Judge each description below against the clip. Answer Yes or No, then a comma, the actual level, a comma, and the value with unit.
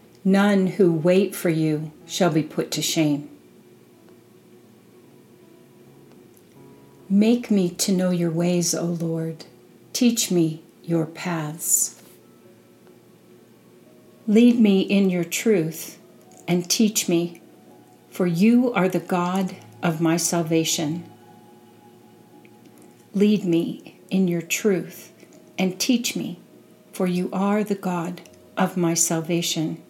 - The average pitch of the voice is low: No, medium, 175 Hz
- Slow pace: Yes, slow, 110 wpm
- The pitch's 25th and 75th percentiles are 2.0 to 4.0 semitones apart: Yes, average, 2.9 semitones